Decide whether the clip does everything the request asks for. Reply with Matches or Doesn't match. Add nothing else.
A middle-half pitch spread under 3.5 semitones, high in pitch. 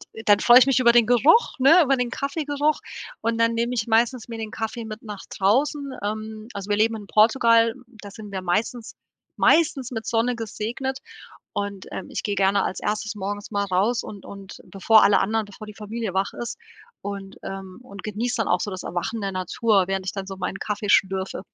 Matches